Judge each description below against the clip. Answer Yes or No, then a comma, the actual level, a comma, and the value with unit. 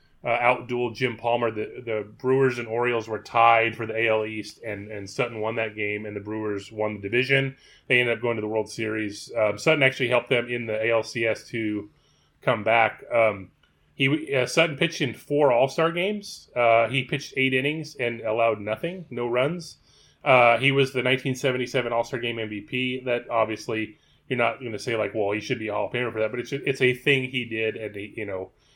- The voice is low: Yes, low, 120 Hz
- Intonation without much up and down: No, average, 3.3 semitones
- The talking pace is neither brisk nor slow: No, fast, 215 wpm